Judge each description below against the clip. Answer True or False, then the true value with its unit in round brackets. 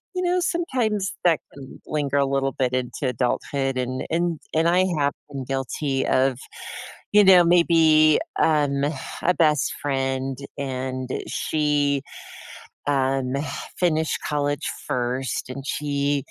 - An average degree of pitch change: True (3.2 semitones)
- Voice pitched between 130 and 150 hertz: True (140 Hz)